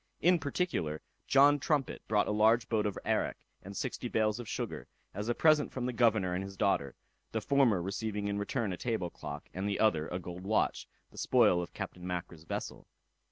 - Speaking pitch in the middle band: No, low, 105 Hz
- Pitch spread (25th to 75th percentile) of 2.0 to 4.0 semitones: No, average, 4.8 semitones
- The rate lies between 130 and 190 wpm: No, average, 200 wpm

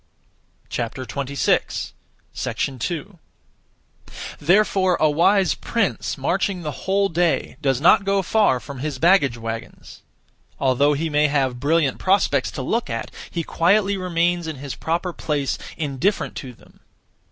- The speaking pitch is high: No, medium, 155 Hz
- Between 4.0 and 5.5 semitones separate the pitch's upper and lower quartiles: Yes, average, 5.2 semitones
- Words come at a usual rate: No, slow, 125 wpm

